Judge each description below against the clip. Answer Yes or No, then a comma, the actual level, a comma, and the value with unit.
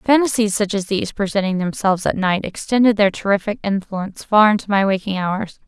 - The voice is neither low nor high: No, high, 200 Hz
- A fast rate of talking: No, average, 180 wpm